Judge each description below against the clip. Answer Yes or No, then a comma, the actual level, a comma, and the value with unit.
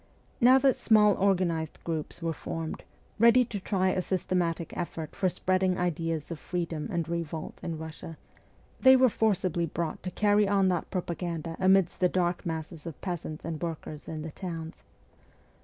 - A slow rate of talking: No, average, 160 wpm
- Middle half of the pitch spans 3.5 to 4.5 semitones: No, narrow, 2.6 semitones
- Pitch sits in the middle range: Yes, medium, 175 Hz